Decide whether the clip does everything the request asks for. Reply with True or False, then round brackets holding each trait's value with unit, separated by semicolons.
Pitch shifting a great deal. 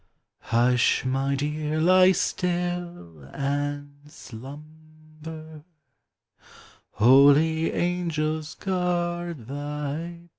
False (3.4 semitones)